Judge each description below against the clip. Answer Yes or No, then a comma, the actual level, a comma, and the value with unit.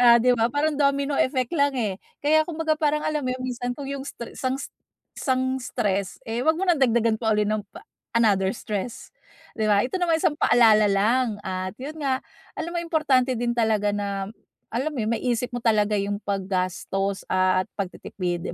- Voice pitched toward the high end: Yes, high, 235 Hz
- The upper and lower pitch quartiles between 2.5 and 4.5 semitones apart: No, average, 5.3 semitones